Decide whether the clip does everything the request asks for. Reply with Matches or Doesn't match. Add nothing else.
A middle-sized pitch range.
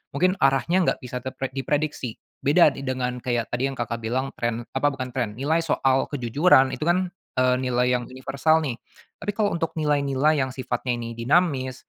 Matches